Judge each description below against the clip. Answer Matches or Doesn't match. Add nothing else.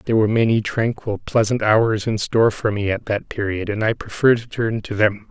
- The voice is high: Doesn't match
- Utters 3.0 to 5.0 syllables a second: Doesn't match